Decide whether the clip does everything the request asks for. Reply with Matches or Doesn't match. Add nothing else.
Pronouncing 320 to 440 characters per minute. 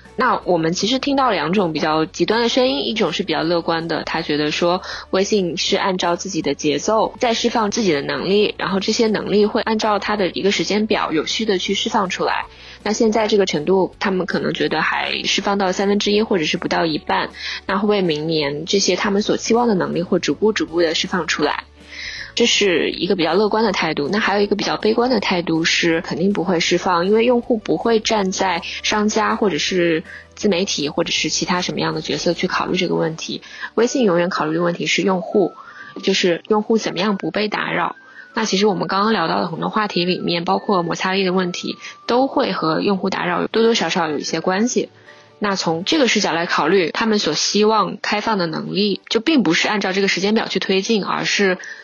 Matches